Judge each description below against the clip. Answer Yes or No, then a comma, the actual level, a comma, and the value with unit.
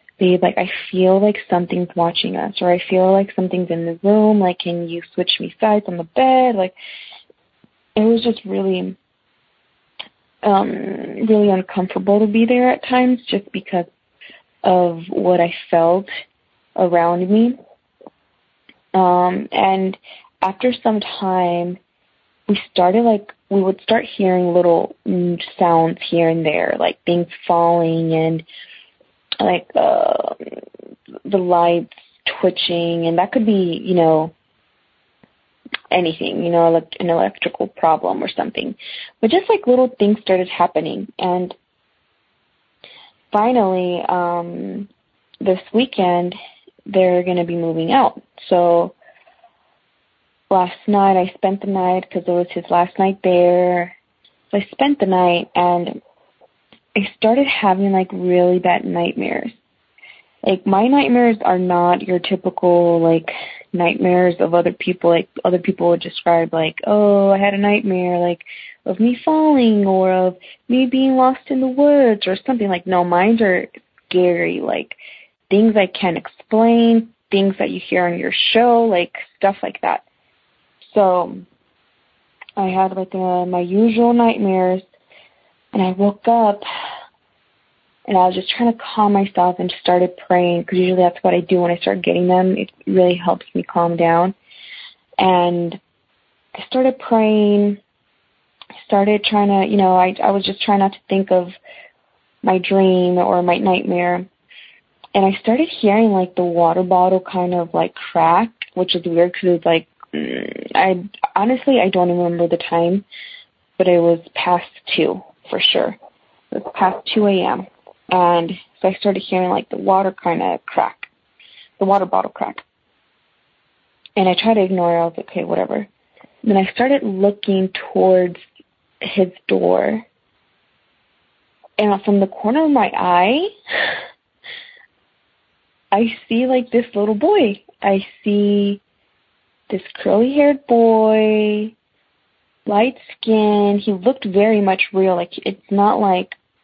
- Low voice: No, high, 190 Hz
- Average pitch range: Yes, average, 3.2 semitones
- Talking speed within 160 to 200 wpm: No, average, 145 wpm